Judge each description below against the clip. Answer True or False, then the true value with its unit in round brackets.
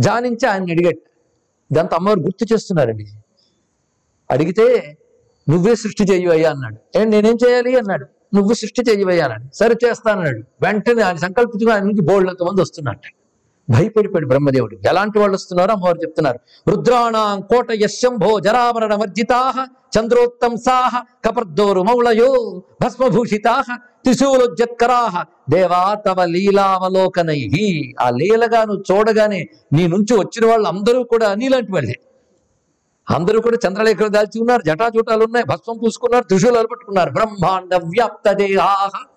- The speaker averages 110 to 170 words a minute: True (115 wpm)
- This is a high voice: True (210 Hz)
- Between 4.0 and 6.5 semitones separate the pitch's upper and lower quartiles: True (4.8 semitones)